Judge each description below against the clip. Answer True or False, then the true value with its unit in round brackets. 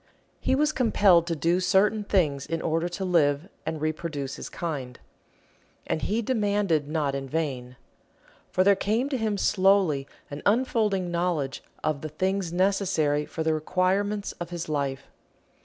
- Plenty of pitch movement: False (4.9 semitones)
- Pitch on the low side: False (175 Hz)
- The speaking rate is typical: True (155 wpm)